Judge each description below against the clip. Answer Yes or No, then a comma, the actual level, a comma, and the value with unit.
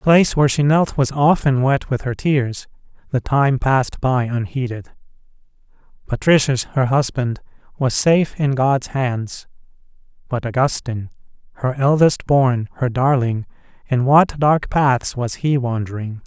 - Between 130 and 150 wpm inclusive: Yes, average, 140 wpm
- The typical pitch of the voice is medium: No, low, 130 Hz